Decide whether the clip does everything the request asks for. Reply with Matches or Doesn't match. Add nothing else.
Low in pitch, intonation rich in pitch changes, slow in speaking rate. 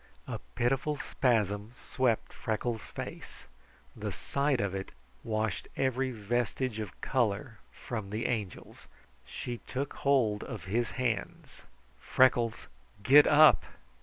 Doesn't match